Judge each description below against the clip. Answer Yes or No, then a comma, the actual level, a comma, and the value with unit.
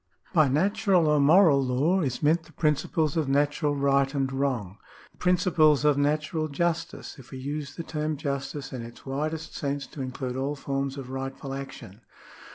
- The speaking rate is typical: Yes, average, 175 wpm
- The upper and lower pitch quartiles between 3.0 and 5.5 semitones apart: No, narrow, 2.5 semitones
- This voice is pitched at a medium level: Yes, medium, 145 Hz